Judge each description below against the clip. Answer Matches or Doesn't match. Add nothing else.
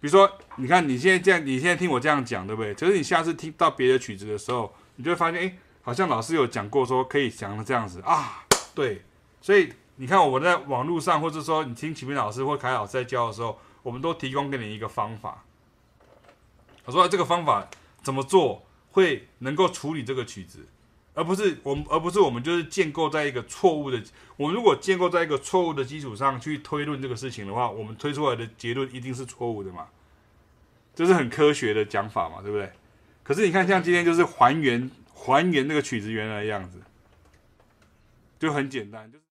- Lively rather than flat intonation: Matches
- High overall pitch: Doesn't match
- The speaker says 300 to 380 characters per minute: Matches